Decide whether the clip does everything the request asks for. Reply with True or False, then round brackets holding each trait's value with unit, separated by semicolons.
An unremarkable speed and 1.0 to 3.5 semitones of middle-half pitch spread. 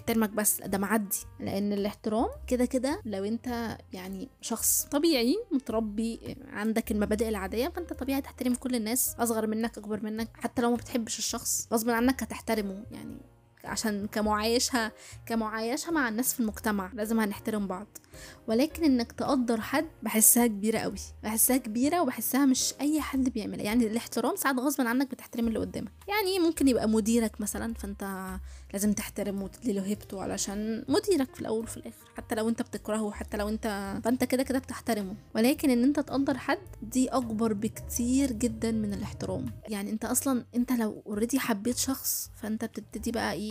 False (165 wpm; 2.9 semitones)